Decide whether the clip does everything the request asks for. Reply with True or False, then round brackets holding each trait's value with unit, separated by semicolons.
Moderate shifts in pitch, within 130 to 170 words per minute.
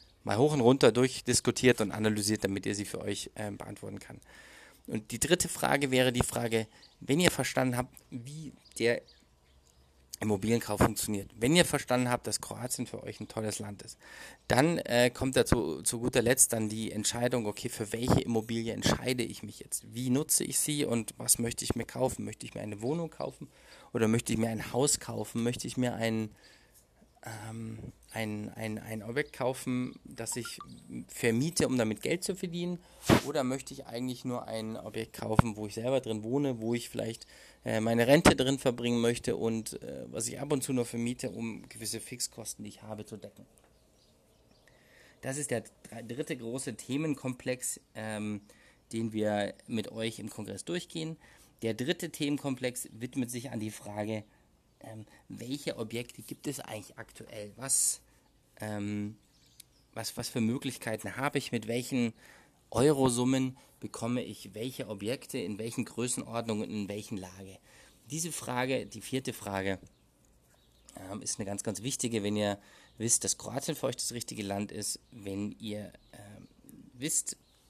True (3.0 semitones; 165 wpm)